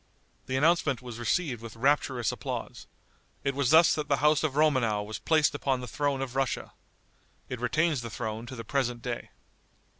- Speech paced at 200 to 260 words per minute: No, average, 180 wpm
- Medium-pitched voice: No, low, 130 Hz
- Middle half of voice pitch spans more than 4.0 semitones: No, average, 3.7 semitones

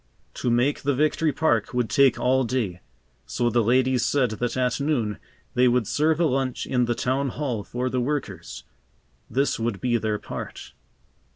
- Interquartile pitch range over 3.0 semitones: No, narrow, 2.6 semitones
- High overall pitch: No, low, 125 Hz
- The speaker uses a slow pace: No, average, 175 wpm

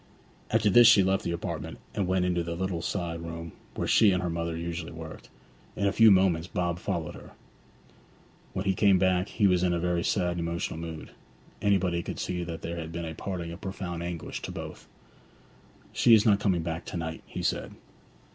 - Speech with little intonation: Yes, narrow, 2.3 semitones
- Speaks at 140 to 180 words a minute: No, fast, 205 wpm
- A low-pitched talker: Yes, very low, 90 Hz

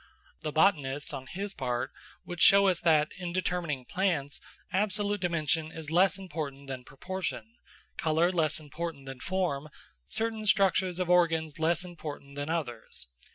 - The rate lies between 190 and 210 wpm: No, average, 145 wpm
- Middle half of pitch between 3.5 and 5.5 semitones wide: Yes, average, 4.3 semitones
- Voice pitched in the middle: Yes, medium, 165 Hz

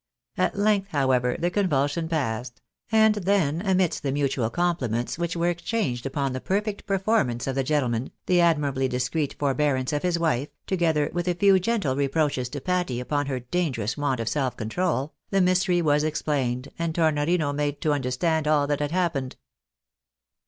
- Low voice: No, medium, 150 Hz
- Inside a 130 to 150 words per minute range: No, average, 175 wpm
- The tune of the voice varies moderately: Yes, average, 4.9 semitones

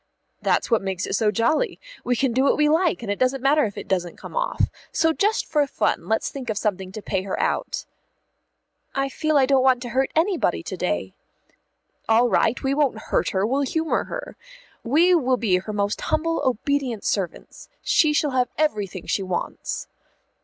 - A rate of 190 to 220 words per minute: Yes, average, 195 wpm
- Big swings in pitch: Yes, wide, 6.3 semitones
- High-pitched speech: Yes, very high, 255 Hz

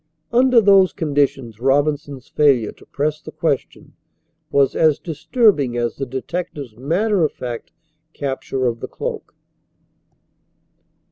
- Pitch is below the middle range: No, medium, 145 Hz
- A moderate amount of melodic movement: Yes, average, 4.1 semitones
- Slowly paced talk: Yes, slow, 120 wpm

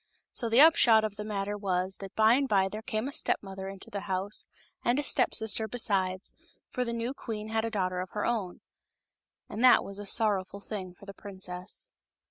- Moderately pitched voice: No, high, 205 Hz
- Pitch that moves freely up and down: No, average, 2.8 semitones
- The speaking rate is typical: No, fast, 215 wpm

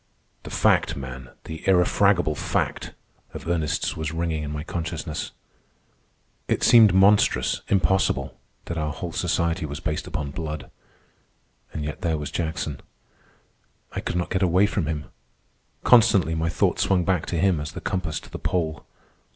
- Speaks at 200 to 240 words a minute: No, average, 155 wpm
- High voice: No, very low, 80 Hz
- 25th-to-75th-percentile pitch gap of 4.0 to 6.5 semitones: No, average, 3.1 semitones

